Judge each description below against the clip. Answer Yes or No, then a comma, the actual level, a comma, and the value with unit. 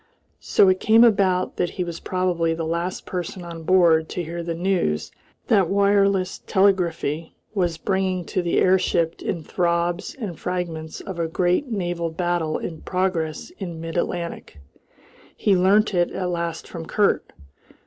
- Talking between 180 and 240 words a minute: No, average, 155 wpm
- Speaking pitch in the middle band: Yes, medium, 175 Hz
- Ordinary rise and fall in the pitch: No, narrow, 2.2 semitones